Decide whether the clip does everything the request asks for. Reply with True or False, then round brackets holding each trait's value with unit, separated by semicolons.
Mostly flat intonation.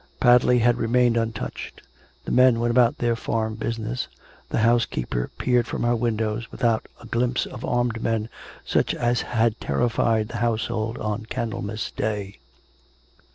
True (1.5 semitones)